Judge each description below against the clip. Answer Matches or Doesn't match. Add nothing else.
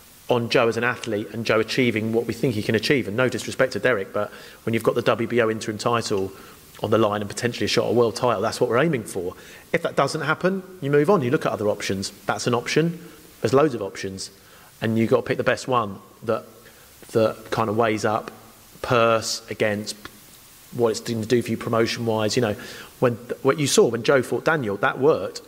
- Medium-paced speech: Doesn't match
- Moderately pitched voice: Doesn't match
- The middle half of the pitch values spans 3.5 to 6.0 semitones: Doesn't match